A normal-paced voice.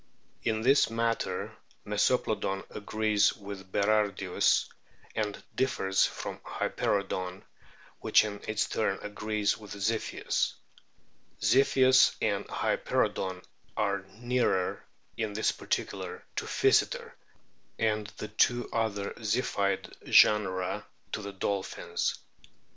No: slow, 100 wpm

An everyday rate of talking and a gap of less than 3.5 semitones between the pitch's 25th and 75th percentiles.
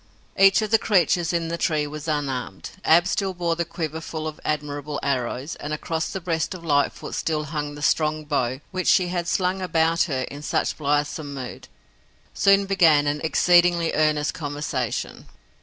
Yes: average, 175 wpm; average, 2.9 semitones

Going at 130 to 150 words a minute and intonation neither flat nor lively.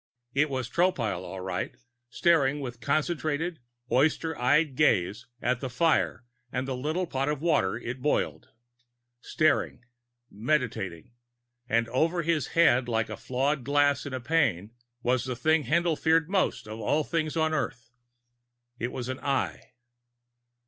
Yes: average, 140 wpm; average, 4.6 semitones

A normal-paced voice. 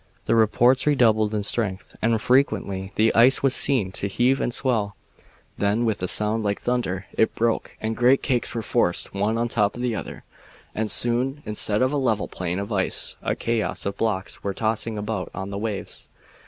Yes: average, 195 wpm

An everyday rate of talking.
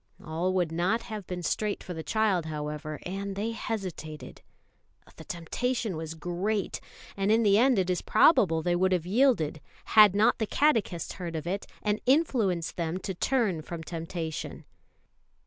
Yes: average, 165 wpm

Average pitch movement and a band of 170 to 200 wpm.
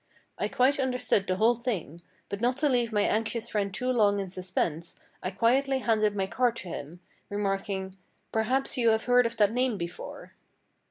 Yes: average, 4.2 semitones; average, 180 wpm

